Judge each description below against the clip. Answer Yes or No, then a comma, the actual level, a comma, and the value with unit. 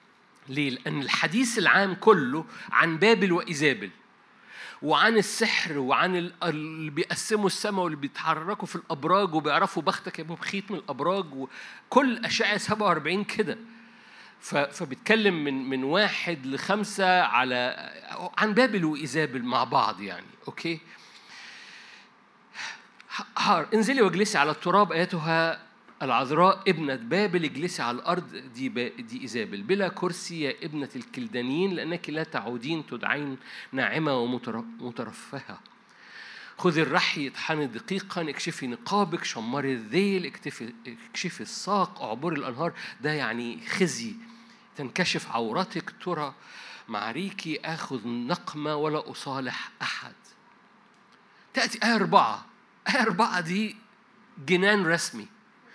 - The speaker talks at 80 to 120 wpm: Yes, average, 105 wpm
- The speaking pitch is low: No, medium, 180 Hz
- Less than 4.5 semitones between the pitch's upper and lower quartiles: No, wide, 5.4 semitones